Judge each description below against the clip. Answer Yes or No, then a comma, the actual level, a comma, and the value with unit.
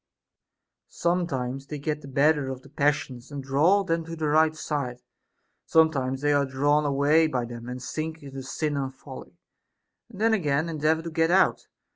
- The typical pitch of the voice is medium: Yes, medium, 145 Hz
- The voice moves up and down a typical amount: Yes, average, 3.0 semitones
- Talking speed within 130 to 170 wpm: No, average, 180 wpm